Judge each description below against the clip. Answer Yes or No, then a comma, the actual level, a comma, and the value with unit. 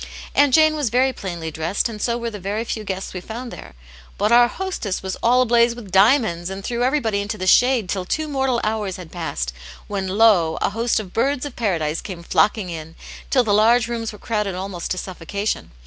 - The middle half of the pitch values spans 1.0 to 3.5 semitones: No, average, 4.3 semitones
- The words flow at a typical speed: No, fast, 215 wpm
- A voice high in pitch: Yes, high, 215 Hz